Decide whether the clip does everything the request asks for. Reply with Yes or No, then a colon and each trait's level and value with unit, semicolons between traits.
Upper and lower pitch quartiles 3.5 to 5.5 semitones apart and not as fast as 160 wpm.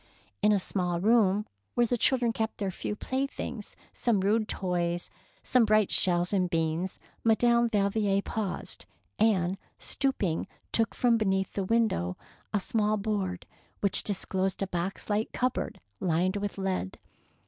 No: average, 3.1 semitones; average, 150 wpm